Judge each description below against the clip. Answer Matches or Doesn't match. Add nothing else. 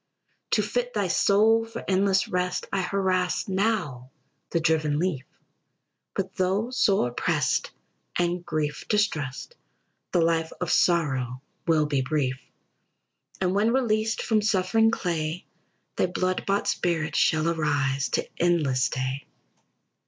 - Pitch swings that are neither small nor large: Matches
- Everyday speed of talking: Doesn't match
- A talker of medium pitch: Matches